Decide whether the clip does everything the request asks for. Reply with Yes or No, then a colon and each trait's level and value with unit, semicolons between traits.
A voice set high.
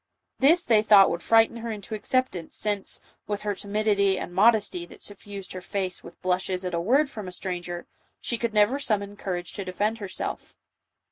Yes: high, 205 Hz